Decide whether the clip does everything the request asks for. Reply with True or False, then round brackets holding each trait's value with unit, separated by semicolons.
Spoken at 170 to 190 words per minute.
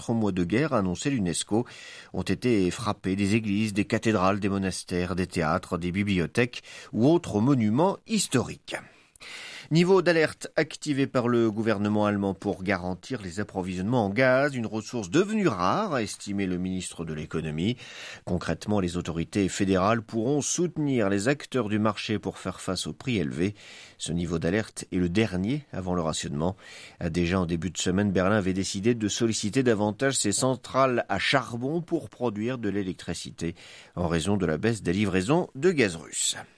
False (160 wpm)